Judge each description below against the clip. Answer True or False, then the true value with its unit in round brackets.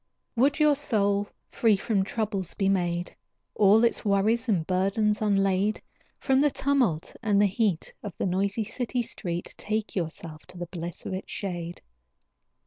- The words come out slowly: False (160 wpm)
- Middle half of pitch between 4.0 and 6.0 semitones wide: False (3.3 semitones)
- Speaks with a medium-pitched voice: False (200 Hz)